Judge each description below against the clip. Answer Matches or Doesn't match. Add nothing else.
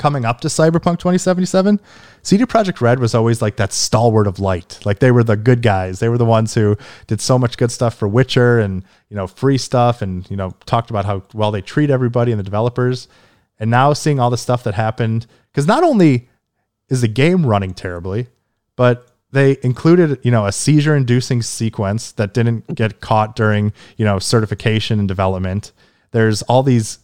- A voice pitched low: Matches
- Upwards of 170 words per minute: Matches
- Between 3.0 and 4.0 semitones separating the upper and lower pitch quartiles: Matches